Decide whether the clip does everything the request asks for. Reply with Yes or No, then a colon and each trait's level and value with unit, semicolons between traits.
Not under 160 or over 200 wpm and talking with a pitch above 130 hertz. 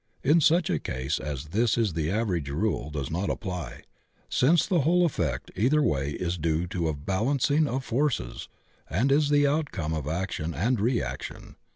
No: average, 170 wpm; very low, 95 Hz